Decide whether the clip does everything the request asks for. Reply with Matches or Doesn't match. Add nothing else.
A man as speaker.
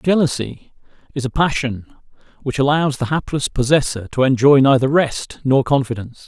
Matches